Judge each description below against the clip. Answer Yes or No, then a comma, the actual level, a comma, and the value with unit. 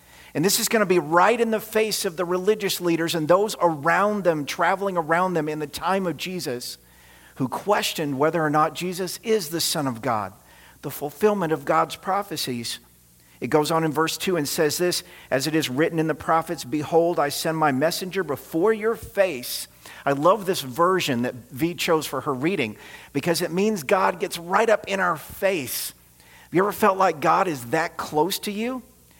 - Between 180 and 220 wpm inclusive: Yes, average, 200 wpm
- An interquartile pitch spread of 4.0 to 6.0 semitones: Yes, average, 4.9 semitones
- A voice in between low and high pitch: Yes, medium, 165 Hz